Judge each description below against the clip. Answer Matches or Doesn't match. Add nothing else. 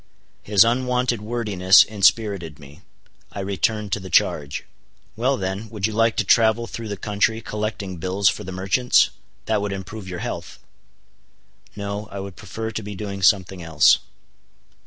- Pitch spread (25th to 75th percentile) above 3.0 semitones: Doesn't match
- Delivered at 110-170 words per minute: Matches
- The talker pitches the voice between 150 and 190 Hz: Doesn't match